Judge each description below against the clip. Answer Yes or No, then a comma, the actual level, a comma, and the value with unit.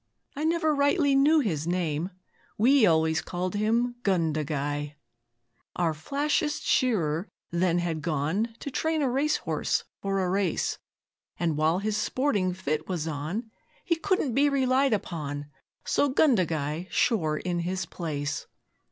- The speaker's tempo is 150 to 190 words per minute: No, slow, 135 wpm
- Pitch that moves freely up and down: Yes, wide, 8.6 semitones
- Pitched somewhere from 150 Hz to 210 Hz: Yes, medium, 185 Hz